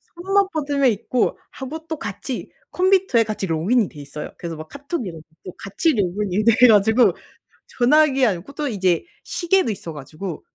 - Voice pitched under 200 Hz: No, high, 230 Hz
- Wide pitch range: Yes, wide, 7.9 semitones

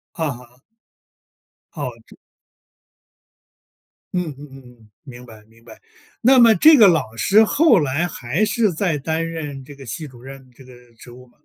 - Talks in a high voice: No, medium, 145 Hz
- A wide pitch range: Yes, wide, 6.2 semitones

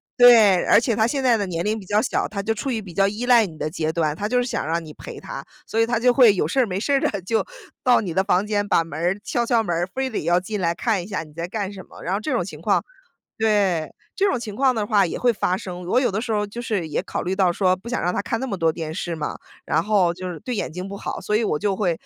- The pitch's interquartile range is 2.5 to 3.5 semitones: No, average, 4.5 semitones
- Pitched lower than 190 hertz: No, high, 200 Hz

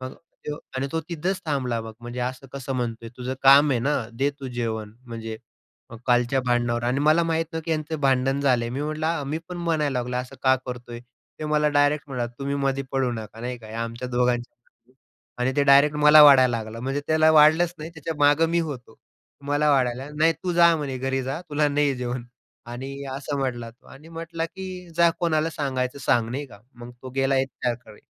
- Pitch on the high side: No, low, 135 Hz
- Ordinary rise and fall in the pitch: Yes, average, 3.6 semitones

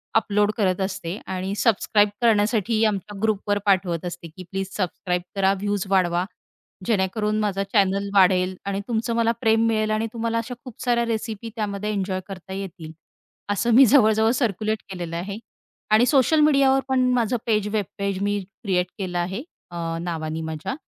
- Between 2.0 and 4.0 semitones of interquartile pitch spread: Yes, average, 3.0 semitones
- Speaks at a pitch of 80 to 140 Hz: No, high, 205 Hz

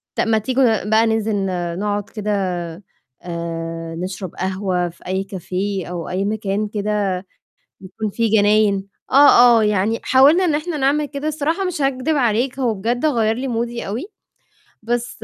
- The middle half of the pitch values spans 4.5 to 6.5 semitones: Yes, average, 4.8 semitones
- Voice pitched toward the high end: Yes, high, 215 Hz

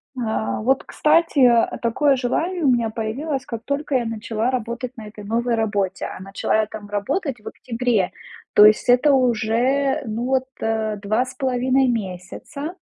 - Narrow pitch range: No, average, 3.5 semitones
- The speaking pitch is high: Yes, high, 240 Hz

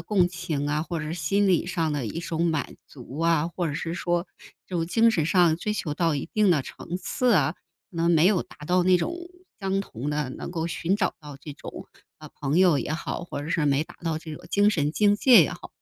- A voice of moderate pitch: Yes, medium, 165 Hz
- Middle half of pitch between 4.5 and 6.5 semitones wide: No, average, 3.3 semitones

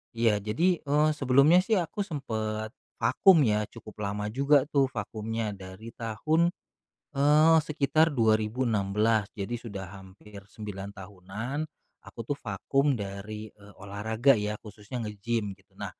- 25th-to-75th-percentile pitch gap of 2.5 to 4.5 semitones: No, average, 4.9 semitones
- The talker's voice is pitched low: Yes, low, 110 Hz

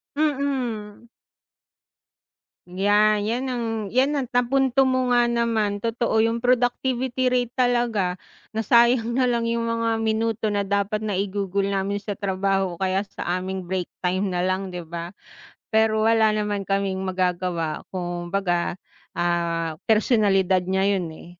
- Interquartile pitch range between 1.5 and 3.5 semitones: No, average, 3.9 semitones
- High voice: Yes, high, 205 Hz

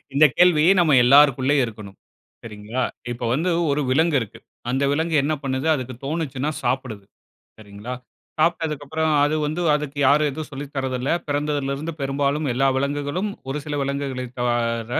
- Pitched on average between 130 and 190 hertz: Yes, medium, 140 Hz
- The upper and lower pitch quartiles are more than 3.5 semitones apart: No, average, 2.8 semitones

